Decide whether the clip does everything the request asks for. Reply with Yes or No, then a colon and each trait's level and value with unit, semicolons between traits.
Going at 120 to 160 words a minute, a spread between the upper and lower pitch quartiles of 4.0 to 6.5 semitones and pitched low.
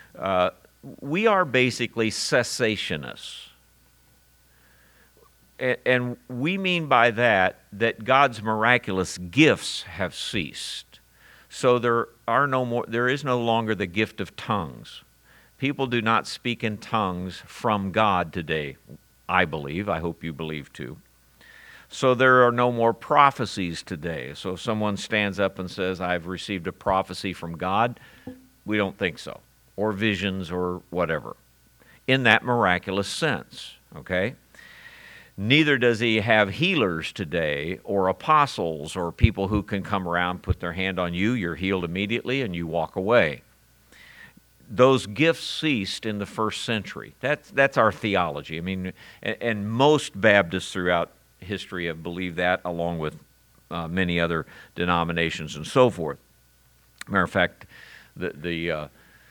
Yes: average, 145 wpm; wide, 5.4 semitones; low, 100 Hz